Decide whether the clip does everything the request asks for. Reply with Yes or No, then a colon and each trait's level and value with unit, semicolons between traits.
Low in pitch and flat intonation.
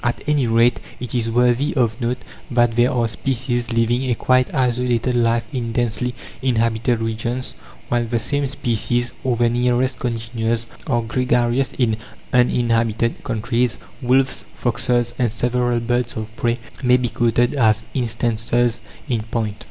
Yes: low, 120 Hz; narrow, 1.3 semitones